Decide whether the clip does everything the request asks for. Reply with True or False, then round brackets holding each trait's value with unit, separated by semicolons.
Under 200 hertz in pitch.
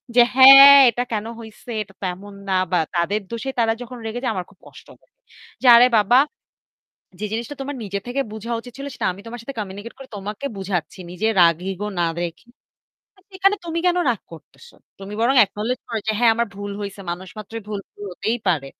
False (220 Hz)